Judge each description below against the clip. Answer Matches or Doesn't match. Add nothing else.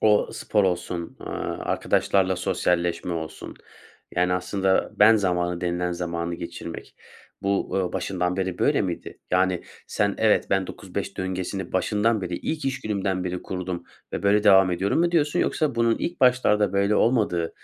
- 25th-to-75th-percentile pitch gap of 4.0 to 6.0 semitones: Doesn't match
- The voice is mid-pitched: Doesn't match